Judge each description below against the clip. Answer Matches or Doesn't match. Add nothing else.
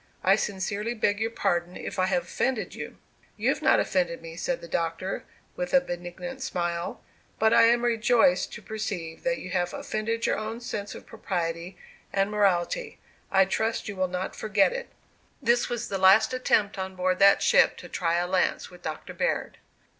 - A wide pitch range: Doesn't match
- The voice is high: Matches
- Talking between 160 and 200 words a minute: Matches